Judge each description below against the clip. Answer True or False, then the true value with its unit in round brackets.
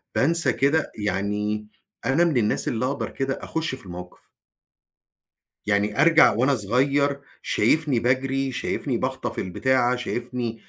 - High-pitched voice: False (125 Hz)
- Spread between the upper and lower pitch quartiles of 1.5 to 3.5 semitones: False (4.7 semitones)